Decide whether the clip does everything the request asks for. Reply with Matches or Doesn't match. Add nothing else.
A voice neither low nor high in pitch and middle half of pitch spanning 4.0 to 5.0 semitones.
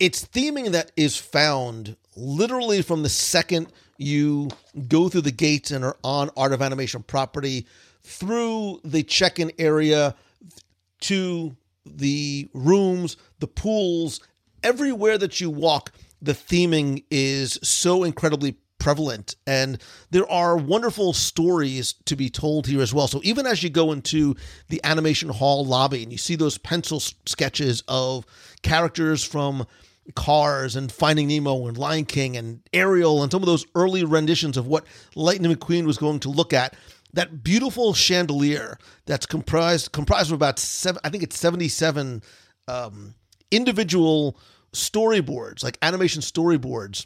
Matches